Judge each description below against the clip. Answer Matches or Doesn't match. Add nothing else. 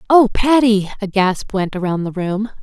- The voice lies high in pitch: Matches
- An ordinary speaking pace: Matches